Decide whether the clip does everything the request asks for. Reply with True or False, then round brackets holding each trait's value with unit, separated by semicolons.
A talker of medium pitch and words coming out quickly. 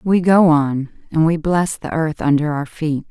True (155 Hz; 215 wpm)